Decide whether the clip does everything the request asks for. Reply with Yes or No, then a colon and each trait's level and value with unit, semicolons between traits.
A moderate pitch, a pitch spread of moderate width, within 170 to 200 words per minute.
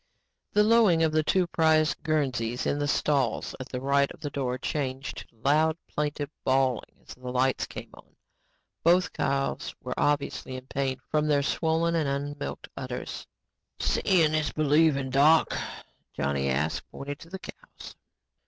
No: medium, 145 Hz; average, 3.0 semitones; average, 155 wpm